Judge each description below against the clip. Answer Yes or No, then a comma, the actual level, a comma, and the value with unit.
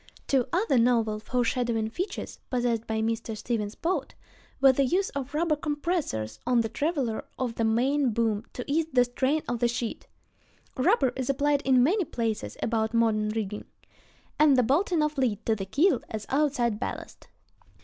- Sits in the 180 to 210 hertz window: No, high, 245 Hz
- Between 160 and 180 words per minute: Yes, average, 170 wpm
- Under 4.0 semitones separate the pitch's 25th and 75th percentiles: No, average, 4.4 semitones